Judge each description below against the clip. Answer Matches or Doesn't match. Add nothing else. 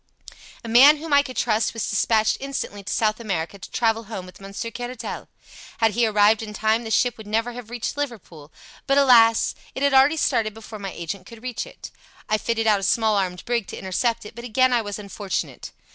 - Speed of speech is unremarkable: Doesn't match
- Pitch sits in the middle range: Doesn't match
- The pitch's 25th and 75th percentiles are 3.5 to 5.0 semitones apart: Doesn't match